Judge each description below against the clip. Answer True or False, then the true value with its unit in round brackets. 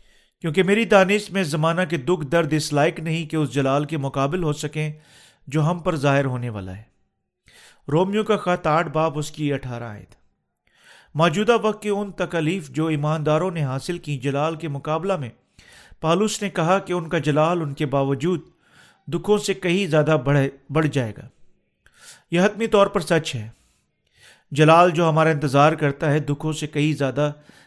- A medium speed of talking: True (180 wpm)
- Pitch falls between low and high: True (155 Hz)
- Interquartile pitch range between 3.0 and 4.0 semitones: True (3.6 semitones)